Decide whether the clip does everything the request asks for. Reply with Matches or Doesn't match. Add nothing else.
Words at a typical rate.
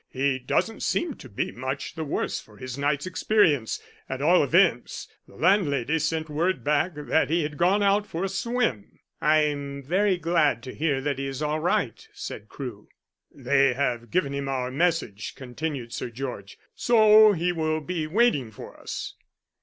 Matches